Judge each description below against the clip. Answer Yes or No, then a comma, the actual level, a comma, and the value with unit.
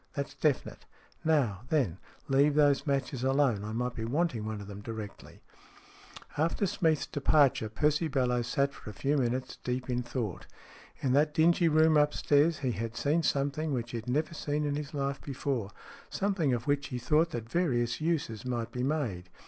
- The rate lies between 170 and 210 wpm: Yes, average, 180 wpm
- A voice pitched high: No, low, 135 Hz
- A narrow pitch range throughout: No, average, 4.0 semitones